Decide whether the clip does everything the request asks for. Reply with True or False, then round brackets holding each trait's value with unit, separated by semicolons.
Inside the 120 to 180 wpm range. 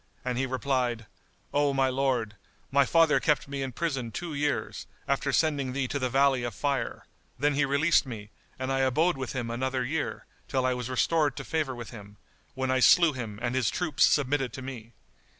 False (200 wpm)